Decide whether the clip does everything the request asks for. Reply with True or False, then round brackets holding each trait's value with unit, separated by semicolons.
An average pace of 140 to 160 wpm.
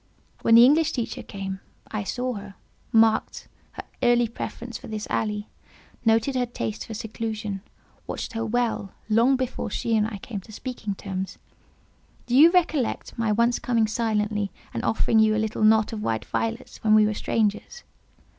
False (170 wpm)